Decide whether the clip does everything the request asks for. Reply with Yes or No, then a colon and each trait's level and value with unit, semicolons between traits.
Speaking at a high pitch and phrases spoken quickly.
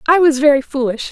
Yes: very high, 285 Hz; fast, 215 wpm